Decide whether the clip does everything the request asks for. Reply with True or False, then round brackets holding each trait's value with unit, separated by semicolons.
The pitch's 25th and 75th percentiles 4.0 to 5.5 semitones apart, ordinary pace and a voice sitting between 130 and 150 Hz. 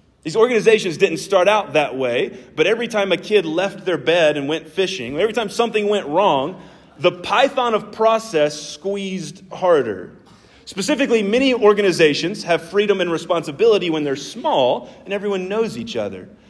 False (4.8 semitones; 160 wpm; 195 Hz)